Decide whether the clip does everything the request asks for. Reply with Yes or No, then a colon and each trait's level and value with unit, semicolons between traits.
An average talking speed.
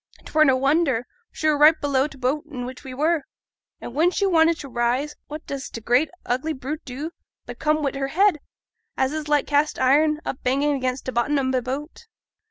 No: fast, 215 wpm